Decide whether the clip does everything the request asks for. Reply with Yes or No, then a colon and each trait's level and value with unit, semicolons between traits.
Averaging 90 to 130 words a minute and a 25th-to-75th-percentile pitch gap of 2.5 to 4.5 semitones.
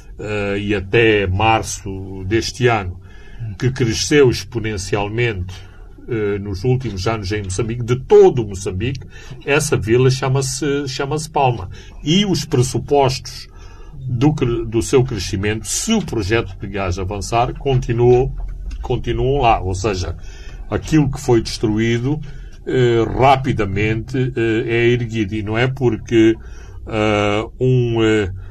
Yes: slow, 120 wpm; average, 3.9 semitones